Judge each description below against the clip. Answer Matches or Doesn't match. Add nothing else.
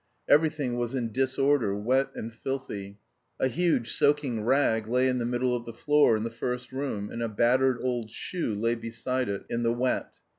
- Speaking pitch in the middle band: Doesn't match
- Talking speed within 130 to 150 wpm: Doesn't match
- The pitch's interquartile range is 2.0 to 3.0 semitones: Matches